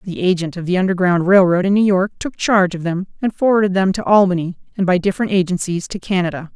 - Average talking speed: No, fast, 230 wpm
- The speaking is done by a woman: Yes, female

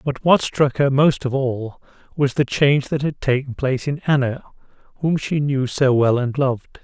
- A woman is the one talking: No, male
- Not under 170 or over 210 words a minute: Yes, average, 200 wpm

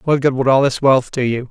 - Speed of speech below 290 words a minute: No, fast, 320 wpm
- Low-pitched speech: Yes, low, 130 Hz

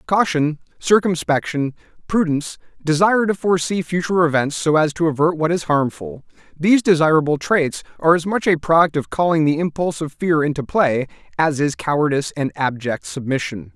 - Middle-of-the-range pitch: Yes, medium, 160 Hz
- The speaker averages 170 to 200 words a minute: No, average, 160 wpm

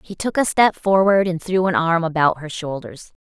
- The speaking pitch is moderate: Yes, medium, 175 Hz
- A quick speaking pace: Yes, fast, 225 wpm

